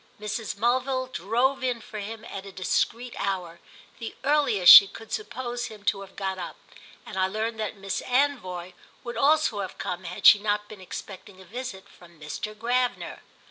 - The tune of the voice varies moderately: Yes, average, 4.3 semitones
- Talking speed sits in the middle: Yes, average, 175 wpm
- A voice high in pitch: Yes, high, 210 Hz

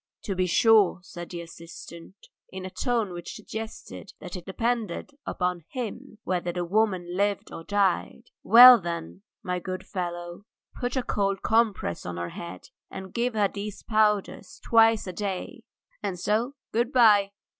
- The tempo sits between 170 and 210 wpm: No, average, 155 wpm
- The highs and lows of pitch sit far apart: No, average, 3.9 semitones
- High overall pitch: Yes, high, 195 Hz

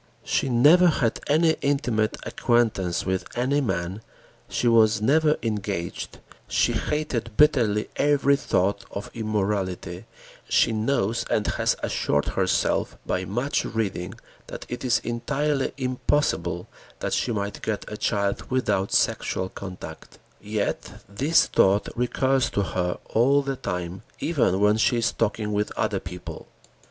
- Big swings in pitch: No, average, 5.0 semitones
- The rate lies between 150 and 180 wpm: No, slow, 135 wpm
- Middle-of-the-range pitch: No, low, 110 Hz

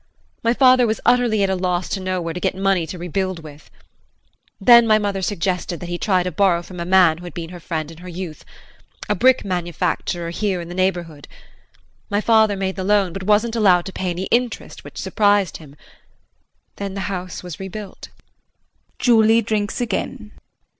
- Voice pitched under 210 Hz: Yes, high, 190 Hz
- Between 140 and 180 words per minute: No, average, 190 wpm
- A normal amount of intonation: Yes, average, 3.1 semitones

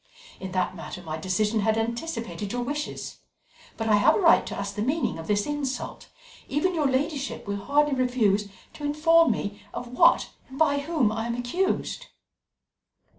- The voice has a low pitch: No, high, 245 Hz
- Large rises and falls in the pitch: Yes, wide, 6.0 semitones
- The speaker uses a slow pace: No, average, 175 wpm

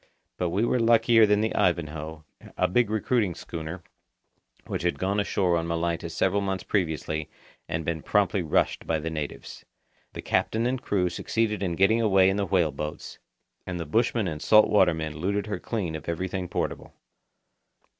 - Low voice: Yes, very low, 90 Hz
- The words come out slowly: No, average, 175 wpm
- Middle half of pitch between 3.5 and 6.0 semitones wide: Yes, average, 4.2 semitones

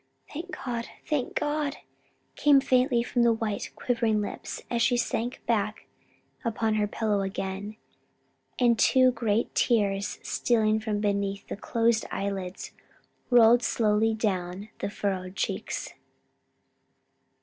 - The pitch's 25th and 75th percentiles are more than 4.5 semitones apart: No, average, 2.9 semitones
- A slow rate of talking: Yes, slow, 120 wpm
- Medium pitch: No, high, 220 Hz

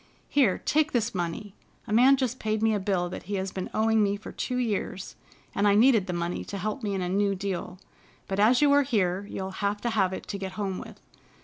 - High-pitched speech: Yes, high, 205 Hz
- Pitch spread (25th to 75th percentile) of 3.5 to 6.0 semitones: No, average, 2.9 semitones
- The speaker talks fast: Yes, fast, 240 wpm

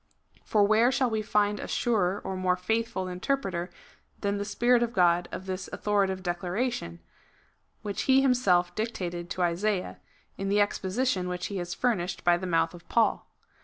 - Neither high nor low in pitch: No, high, 195 Hz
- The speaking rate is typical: Yes, average, 170 wpm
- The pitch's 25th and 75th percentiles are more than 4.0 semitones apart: No, average, 3.7 semitones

